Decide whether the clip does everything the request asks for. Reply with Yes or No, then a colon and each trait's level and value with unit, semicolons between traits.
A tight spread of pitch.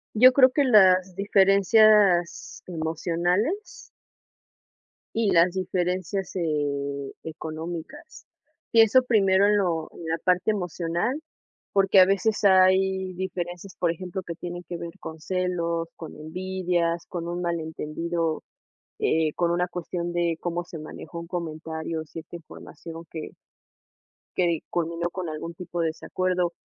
Yes: narrow, 2.3 semitones